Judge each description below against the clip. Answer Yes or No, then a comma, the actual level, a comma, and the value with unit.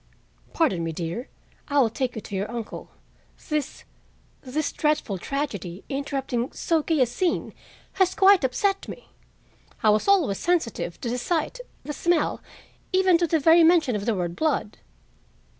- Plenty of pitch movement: Yes, wide, 7.2 semitones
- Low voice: No, very high, 275 Hz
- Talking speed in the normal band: Yes, average, 155 wpm